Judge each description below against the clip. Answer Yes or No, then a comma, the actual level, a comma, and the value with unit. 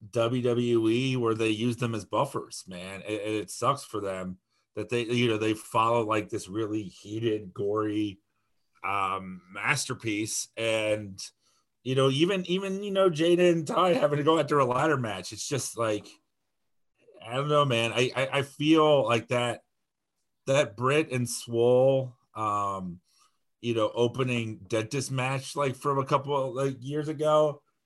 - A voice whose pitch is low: Yes, low, 120 Hz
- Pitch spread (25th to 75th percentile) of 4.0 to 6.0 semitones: Yes, average, 4.3 semitones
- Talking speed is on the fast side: No, average, 160 wpm